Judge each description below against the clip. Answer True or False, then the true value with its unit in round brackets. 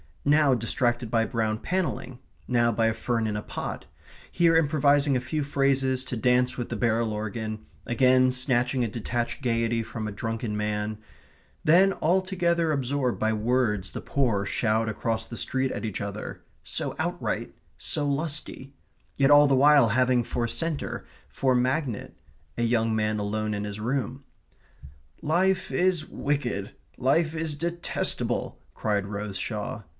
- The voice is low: True (125 Hz)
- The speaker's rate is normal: True (150 wpm)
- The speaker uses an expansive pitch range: False (4.4 semitones)